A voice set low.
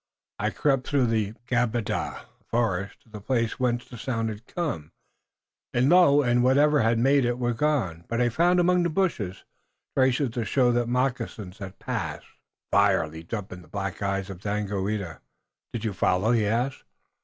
Yes: low, 120 Hz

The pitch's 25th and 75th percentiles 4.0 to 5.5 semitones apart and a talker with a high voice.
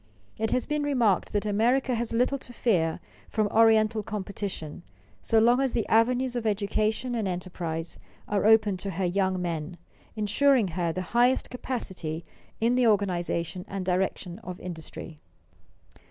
Yes: average, 4.6 semitones; high, 210 Hz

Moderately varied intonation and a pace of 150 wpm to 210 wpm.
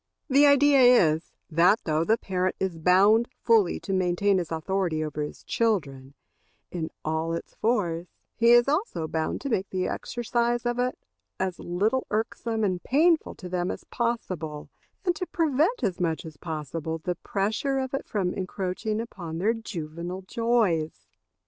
No: wide, 6.0 semitones; average, 160 wpm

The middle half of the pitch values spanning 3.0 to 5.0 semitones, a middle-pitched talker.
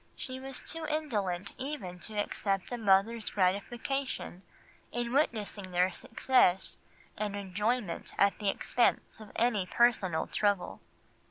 No: average, 4.2 semitones; high, 210 Hz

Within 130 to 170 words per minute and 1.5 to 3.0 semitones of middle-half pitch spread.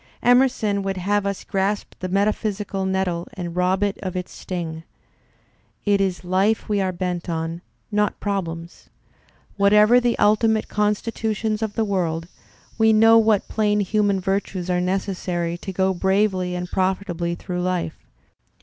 Yes: average, 150 wpm; narrow, 2.6 semitones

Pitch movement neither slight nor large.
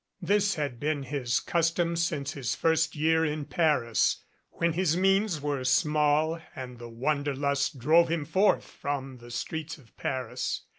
Yes: average, 3.6 semitones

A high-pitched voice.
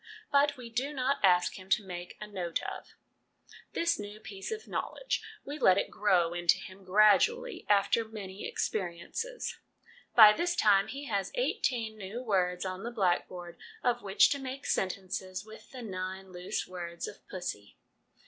Yes: high, 205 Hz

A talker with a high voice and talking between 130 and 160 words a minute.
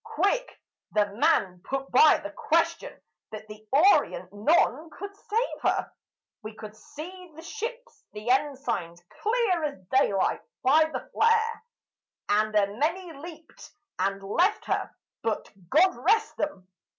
Yes: very high, 300 Hz; slow, 135 wpm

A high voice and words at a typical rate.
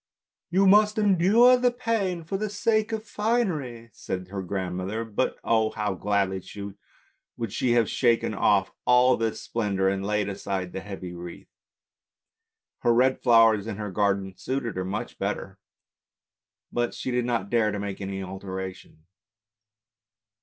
No: low, 110 Hz; average, 155 wpm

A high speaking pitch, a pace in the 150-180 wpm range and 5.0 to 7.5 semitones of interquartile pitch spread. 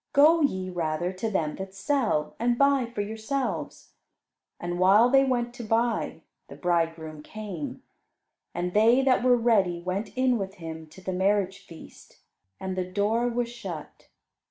Yes: high, 200 Hz; average, 155 wpm; average, 5.3 semitones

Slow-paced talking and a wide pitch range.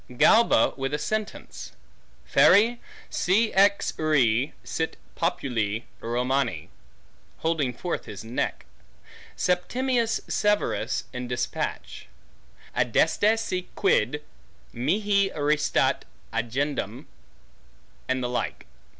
Yes: slow, 90 wpm; wide, 8.3 semitones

